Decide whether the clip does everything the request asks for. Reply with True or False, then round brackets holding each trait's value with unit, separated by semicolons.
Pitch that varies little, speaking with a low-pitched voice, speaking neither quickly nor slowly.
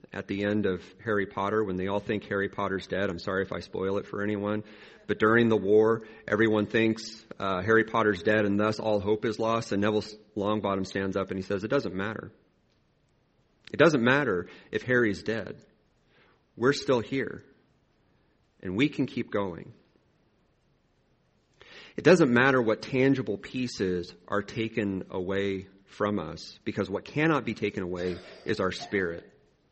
True (2.2 semitones; 105 Hz; 165 wpm)